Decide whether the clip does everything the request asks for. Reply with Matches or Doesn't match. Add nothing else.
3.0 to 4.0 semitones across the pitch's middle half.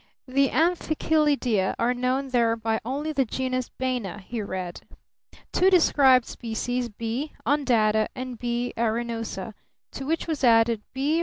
Matches